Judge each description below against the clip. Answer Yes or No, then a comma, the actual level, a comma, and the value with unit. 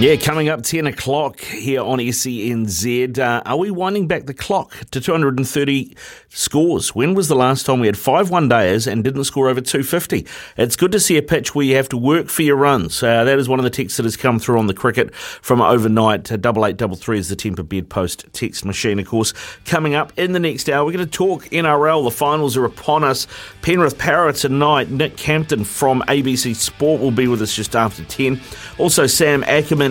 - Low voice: Yes, low, 130 Hz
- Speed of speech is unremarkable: No, fast, 230 wpm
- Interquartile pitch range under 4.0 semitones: No, average, 4.5 semitones